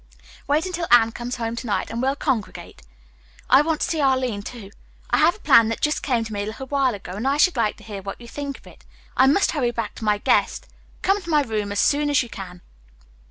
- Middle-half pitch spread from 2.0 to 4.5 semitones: No, average, 4.9 semitones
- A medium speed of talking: No, fast, 255 wpm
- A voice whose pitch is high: Yes, high, 245 Hz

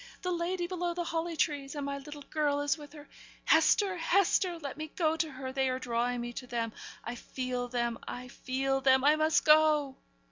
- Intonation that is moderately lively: Yes, average, 3.8 semitones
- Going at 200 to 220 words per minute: Yes, fast, 205 wpm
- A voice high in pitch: Yes, very high, 285 Hz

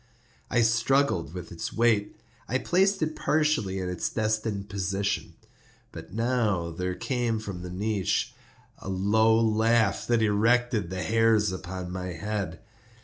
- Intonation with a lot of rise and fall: No, average, 3.6 semitones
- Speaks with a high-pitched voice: No, low, 105 Hz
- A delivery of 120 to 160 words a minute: Yes, average, 145 wpm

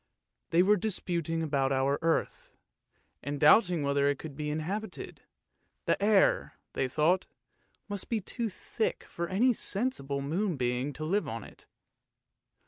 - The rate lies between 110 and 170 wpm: Yes, average, 140 wpm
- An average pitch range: No, wide, 6.1 semitones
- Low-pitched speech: No, medium, 165 Hz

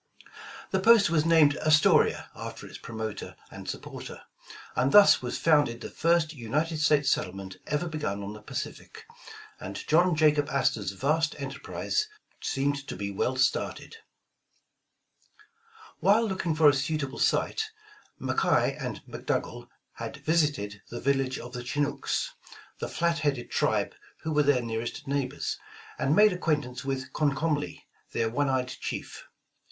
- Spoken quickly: No, average, 140 wpm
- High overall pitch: No, medium, 145 Hz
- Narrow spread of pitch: No, average, 4.0 semitones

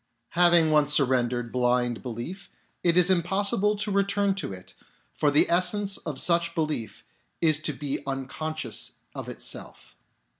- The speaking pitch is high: No, medium, 155 Hz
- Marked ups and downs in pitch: Yes, wide, 5.8 semitones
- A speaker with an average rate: Yes, average, 145 wpm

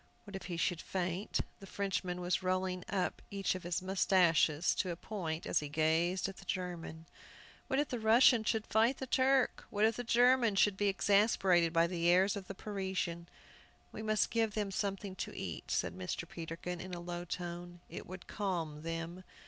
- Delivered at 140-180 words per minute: No, average, 190 wpm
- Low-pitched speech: No, medium, 185 Hz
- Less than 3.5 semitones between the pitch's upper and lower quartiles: Yes, average, 3.1 semitones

